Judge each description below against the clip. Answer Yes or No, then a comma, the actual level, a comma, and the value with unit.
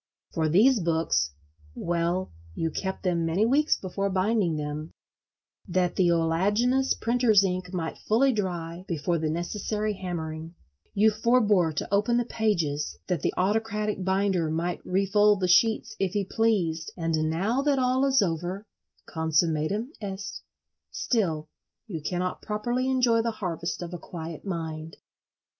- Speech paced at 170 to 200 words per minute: No, slow, 135 wpm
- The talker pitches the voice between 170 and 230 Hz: Yes, medium, 185 Hz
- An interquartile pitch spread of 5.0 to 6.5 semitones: No, average, 4.6 semitones